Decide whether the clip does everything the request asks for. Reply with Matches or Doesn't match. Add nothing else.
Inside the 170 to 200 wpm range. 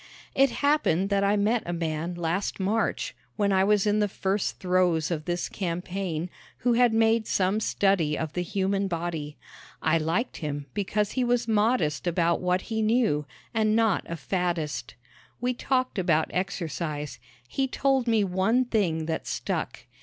Doesn't match